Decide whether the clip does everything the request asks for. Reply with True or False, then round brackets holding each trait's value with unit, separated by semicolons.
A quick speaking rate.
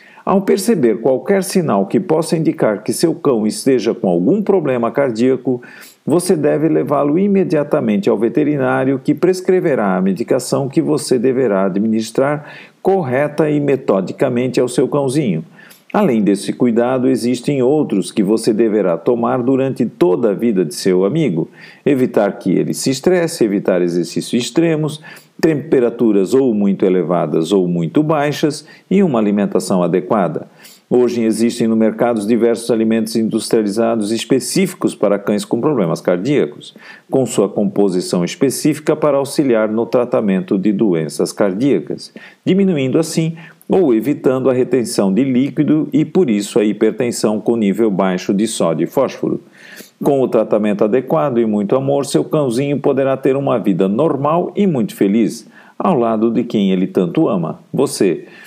False (145 wpm)